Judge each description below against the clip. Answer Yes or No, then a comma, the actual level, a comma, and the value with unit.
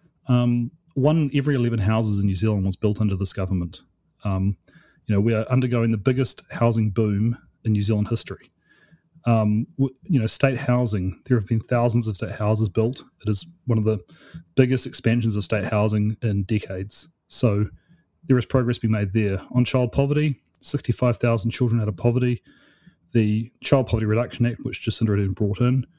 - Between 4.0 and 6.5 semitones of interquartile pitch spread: No, average, 3.2 semitones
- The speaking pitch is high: No, low, 115 Hz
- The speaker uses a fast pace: No, average, 180 wpm